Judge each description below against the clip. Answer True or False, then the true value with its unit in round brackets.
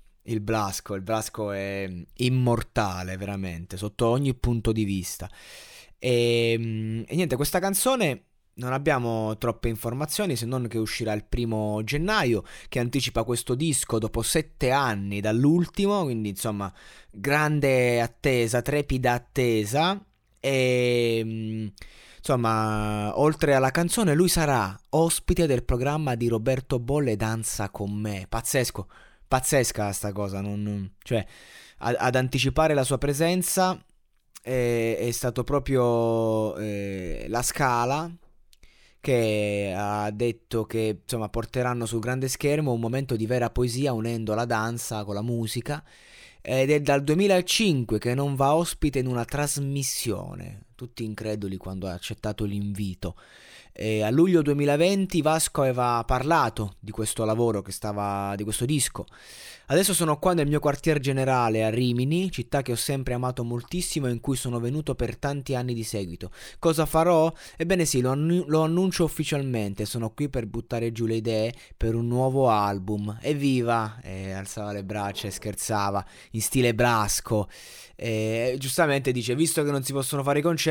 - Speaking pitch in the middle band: False (120 Hz)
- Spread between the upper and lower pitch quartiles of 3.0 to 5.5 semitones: True (4.6 semitones)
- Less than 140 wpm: False (145 wpm)